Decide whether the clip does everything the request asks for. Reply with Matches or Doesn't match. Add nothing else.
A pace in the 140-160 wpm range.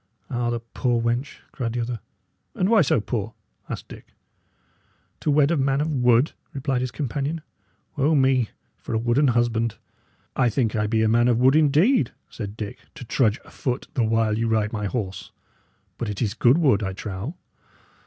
Doesn't match